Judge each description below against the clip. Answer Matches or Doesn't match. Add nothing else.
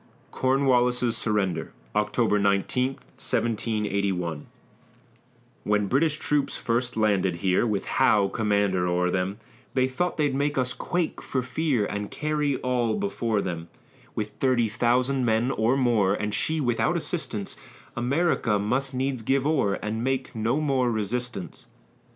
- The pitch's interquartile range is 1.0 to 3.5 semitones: Doesn't match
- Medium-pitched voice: Doesn't match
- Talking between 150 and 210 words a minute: Doesn't match